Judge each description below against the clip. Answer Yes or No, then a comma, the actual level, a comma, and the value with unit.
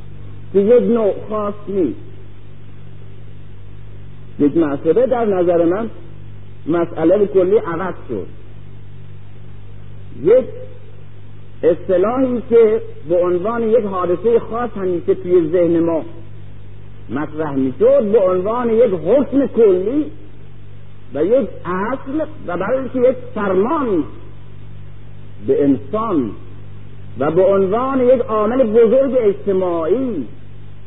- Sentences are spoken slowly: Yes, slow, 95 wpm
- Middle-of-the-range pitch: Yes, medium, 155 Hz